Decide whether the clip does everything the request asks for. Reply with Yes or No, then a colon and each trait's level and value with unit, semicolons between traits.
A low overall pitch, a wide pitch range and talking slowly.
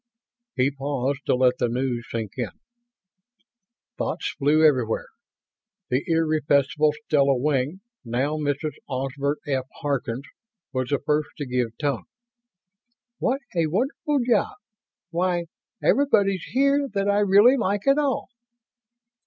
No: medium, 145 Hz; wide, 6.4 semitones; slow, 120 wpm